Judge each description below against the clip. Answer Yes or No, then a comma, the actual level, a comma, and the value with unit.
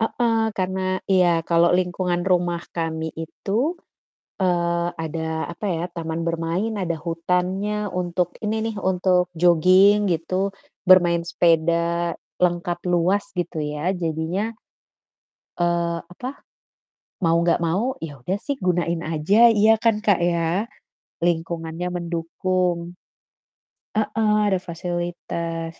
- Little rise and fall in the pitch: Yes, narrow, 1.8 semitones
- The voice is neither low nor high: Yes, medium, 175 Hz